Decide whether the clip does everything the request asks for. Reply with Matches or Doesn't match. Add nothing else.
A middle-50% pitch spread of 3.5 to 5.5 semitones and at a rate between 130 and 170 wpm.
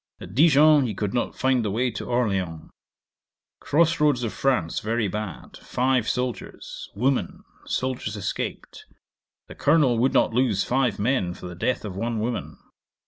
Matches